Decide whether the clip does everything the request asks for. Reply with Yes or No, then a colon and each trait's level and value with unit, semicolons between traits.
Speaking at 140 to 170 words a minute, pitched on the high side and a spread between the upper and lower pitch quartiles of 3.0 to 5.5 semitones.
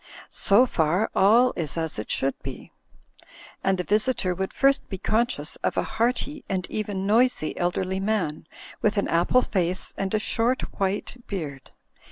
Yes: average, 160 wpm; high, 195 Hz; average, 4.2 semitones